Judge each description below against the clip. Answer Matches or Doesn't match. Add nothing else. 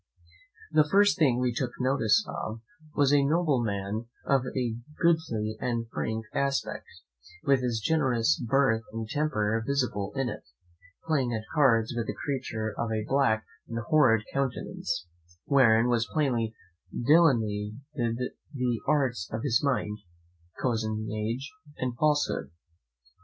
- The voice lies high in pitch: Doesn't match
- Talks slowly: Matches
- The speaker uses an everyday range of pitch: Matches